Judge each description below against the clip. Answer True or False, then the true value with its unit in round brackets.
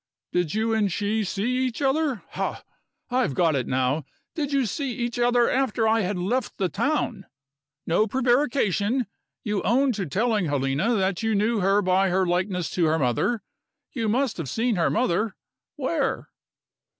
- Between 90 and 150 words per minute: False (165 wpm)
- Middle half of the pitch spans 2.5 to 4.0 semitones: False (5.1 semitones)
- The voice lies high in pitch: True (215 Hz)